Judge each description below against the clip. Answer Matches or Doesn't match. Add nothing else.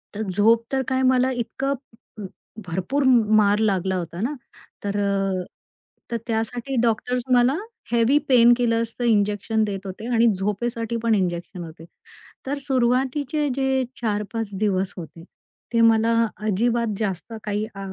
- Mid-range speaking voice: Doesn't match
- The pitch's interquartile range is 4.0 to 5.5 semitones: Doesn't match